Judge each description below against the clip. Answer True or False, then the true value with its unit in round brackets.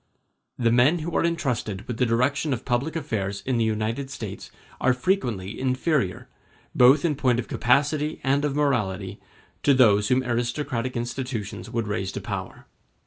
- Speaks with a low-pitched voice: True (125 Hz)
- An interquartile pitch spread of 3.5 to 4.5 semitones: True (4.1 semitones)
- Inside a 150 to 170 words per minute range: True (160 wpm)